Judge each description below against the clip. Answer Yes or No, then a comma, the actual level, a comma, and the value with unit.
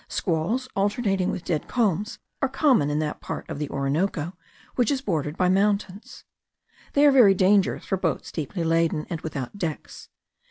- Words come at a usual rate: Yes, average, 165 wpm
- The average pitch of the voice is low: No, medium, 185 Hz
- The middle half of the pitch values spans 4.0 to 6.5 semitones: Yes, average, 4.9 semitones